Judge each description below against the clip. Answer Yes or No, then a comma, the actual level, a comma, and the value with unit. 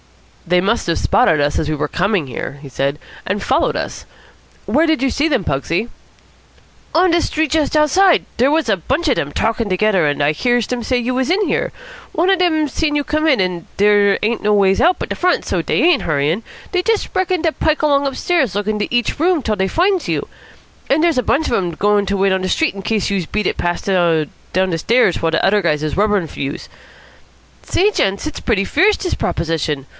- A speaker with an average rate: No, fast, 230 wpm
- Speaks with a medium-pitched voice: No, high, 215 Hz